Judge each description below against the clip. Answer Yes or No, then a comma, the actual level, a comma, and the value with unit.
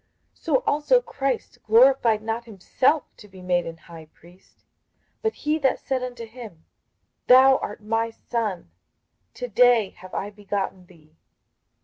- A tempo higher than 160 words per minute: No, average, 145 wpm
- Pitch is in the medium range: No, high, 225 Hz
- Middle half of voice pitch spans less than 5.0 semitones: No, wide, 5.4 semitones